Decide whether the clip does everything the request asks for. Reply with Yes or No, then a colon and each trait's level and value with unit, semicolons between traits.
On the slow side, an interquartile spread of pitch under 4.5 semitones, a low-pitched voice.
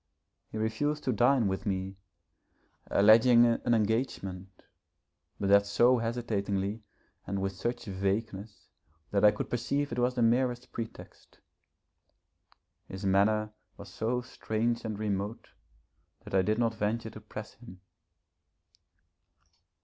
Yes: slow, 125 wpm; average, 3.0 semitones; low, 110 Hz